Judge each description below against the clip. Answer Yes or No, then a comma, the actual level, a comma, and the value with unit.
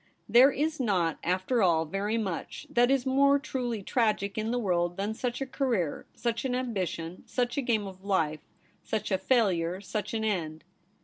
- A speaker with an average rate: Yes, average, 180 wpm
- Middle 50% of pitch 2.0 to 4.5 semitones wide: No, average, 4.9 semitones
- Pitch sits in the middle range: No, high, 215 Hz